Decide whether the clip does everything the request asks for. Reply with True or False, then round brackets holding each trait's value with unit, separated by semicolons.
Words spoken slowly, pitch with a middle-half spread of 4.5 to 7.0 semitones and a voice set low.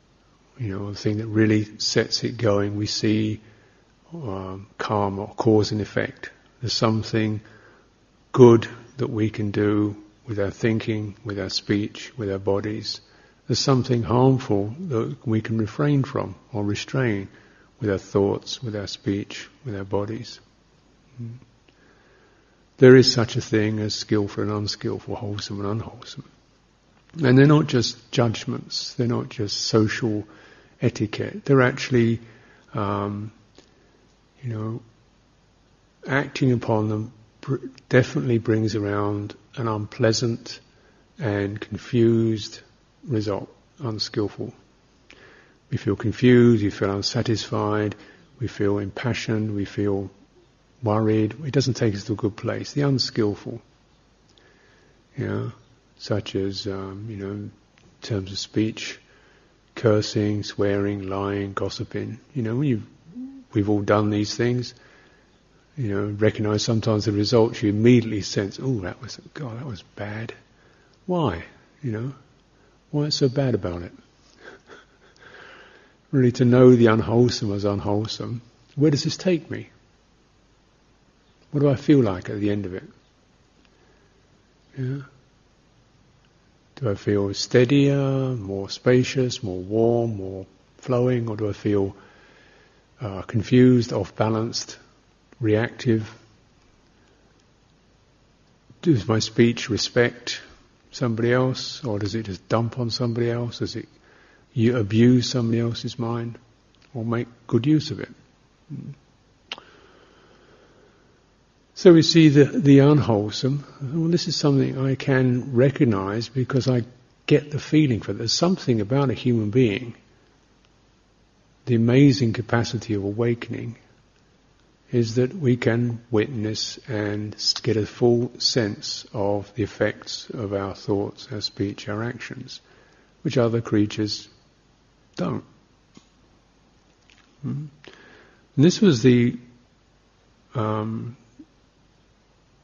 False (120 wpm; 3.3 semitones; 115 Hz)